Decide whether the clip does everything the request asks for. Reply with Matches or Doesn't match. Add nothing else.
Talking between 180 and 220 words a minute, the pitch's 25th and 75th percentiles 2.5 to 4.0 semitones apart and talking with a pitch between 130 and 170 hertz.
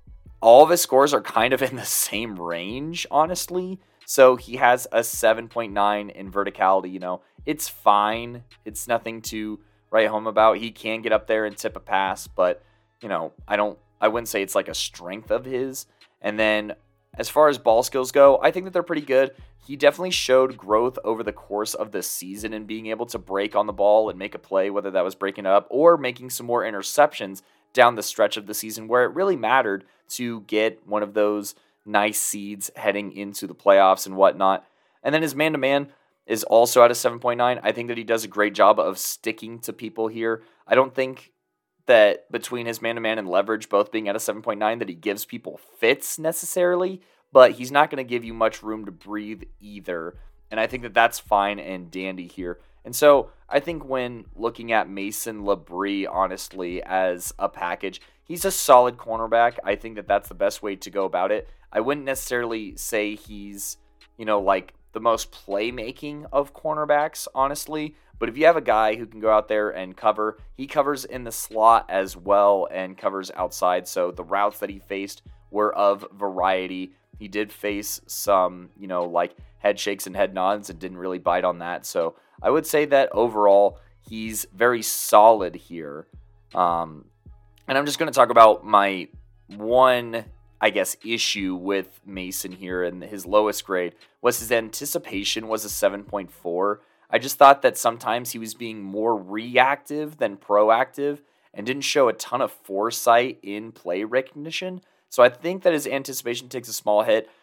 Doesn't match